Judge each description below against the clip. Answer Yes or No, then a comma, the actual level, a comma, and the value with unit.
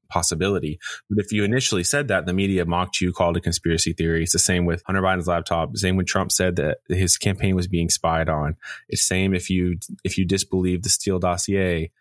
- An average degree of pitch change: No, narrow, 2.1 semitones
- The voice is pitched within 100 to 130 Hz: No, very low, 90 Hz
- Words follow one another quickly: Yes, fast, 220 wpm